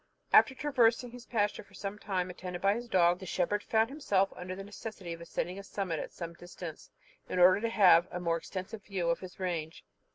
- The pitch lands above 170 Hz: Yes, high, 190 Hz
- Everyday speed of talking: No, fast, 215 wpm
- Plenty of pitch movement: No, average, 2.9 semitones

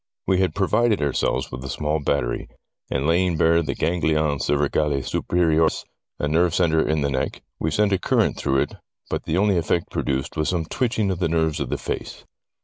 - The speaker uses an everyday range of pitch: Yes, average, 3.3 semitones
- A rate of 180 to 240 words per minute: Yes, average, 200 wpm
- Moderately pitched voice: No, very low, 80 Hz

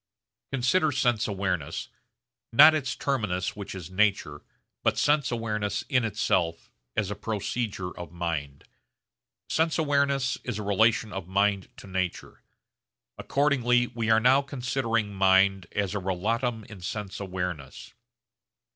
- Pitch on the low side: Yes, low, 105 Hz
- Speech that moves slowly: Yes, slow, 130 wpm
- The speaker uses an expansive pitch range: No, average, 4.6 semitones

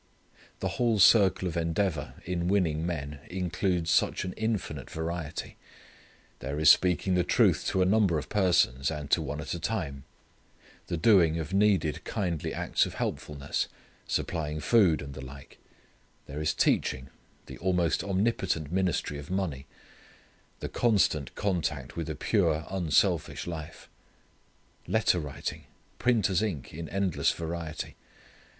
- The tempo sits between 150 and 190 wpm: No, average, 140 wpm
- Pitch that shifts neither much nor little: Yes, average, 3.8 semitones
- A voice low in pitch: Yes, very low, 85 Hz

